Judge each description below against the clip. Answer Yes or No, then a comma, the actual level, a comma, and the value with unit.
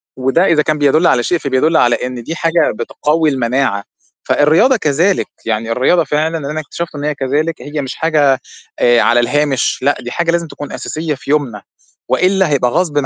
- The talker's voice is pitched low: No, medium, 145 Hz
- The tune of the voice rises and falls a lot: No, average, 3.9 semitones